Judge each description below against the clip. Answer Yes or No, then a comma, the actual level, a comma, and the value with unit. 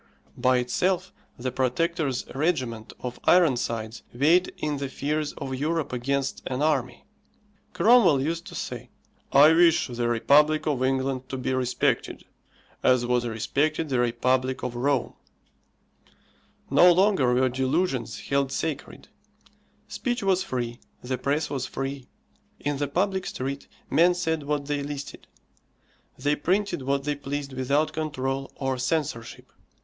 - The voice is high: No, medium, 140 Hz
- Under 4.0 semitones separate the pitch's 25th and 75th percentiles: Yes, average, 3.4 semitones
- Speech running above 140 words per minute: No, slow, 135 wpm